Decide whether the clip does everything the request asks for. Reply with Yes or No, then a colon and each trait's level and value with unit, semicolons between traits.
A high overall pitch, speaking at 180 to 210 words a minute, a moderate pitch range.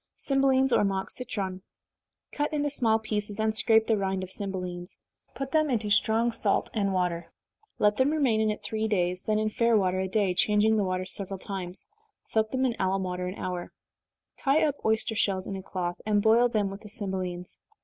Yes: high, 210 Hz; average, 200 wpm; average, 3.1 semitones